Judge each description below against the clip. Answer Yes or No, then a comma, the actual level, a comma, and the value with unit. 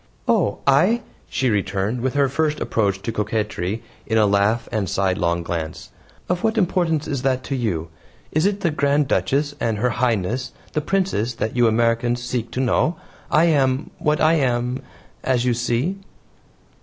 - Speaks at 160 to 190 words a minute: Yes, average, 170 wpm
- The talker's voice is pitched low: Yes, low, 125 Hz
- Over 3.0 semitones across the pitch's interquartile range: Yes, average, 5.2 semitones